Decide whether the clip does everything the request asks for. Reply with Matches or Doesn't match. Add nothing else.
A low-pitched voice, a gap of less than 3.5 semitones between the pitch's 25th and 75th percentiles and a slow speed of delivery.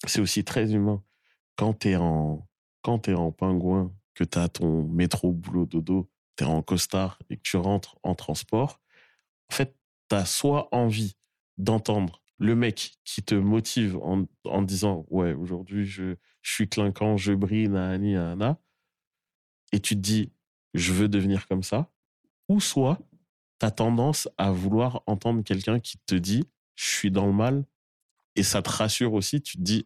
Doesn't match